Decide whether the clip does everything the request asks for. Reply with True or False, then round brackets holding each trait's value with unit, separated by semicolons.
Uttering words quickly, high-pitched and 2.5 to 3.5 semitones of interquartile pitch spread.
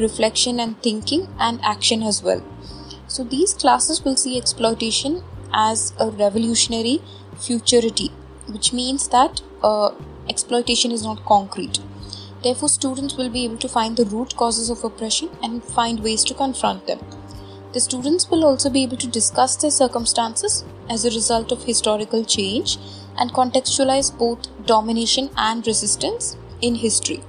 True (145 wpm; 235 Hz; 2.8 semitones)